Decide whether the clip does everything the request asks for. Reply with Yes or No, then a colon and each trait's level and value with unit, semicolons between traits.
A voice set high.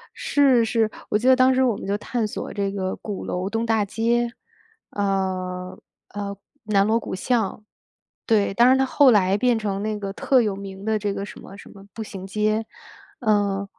Yes: high, 210 Hz